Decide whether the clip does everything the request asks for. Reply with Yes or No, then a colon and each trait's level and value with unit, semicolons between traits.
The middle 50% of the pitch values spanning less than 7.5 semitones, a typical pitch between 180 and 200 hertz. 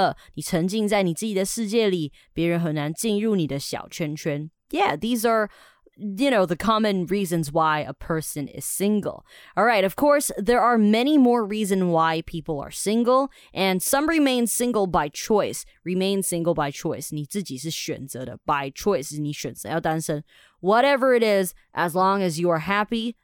Yes: wide, 5.5 semitones; high, 190 Hz